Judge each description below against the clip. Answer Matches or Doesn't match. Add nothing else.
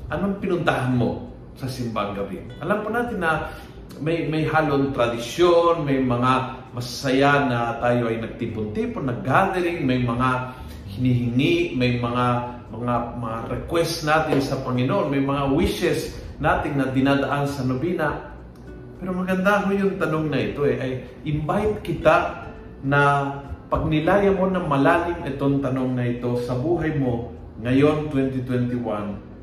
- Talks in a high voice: Doesn't match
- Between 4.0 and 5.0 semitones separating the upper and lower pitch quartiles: Matches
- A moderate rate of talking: Matches